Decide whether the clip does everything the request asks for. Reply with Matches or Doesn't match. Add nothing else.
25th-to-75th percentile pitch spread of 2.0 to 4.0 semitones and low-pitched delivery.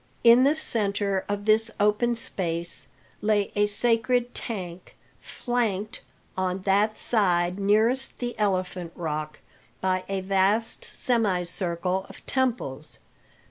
Doesn't match